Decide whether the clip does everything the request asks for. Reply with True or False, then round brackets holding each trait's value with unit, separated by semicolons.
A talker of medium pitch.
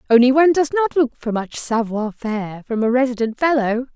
False (250 Hz)